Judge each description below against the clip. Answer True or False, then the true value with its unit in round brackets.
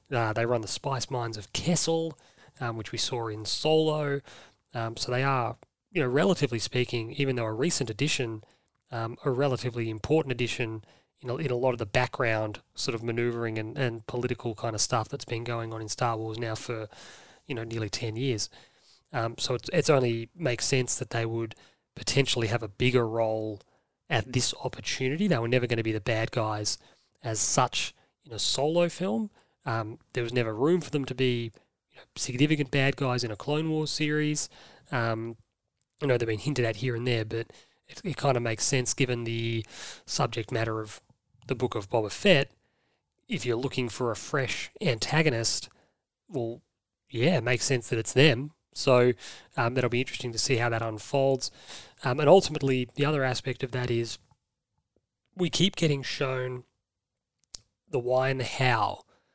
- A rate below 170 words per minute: False (185 wpm)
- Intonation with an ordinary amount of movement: True (3.1 semitones)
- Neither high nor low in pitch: False (125 Hz)